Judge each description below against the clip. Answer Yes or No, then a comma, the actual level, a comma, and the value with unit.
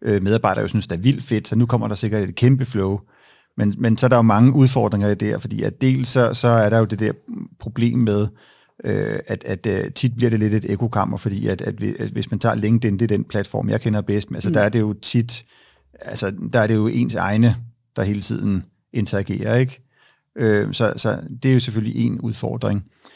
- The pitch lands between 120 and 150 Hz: No, low, 110 Hz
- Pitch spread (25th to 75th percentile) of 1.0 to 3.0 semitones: Yes, narrow, 2.5 semitones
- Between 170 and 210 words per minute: No, fast, 225 wpm